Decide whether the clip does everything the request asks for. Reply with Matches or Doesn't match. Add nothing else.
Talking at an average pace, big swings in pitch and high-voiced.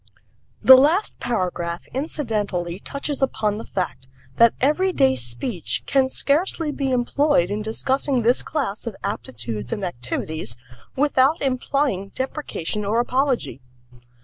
Doesn't match